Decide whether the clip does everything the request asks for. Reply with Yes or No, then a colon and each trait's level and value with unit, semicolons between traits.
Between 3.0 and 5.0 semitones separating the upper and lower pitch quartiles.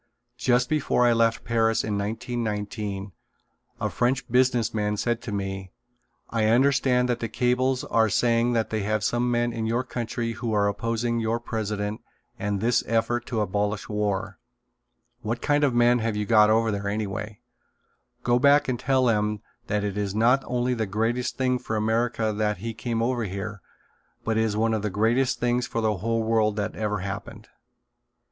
No: narrow, 2.5 semitones